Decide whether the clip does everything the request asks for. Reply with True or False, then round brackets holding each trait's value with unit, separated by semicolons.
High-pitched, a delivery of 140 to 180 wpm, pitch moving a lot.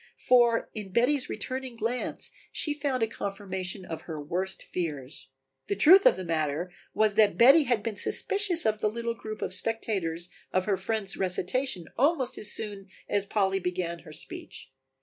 False (205 Hz; 170 wpm; 4.7 semitones)